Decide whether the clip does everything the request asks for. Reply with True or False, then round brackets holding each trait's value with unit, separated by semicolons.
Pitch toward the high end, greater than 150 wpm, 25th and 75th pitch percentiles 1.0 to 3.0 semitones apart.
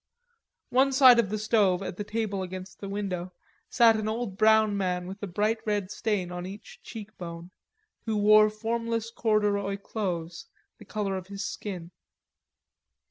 True (205 Hz; 160 wpm; 2.7 semitones)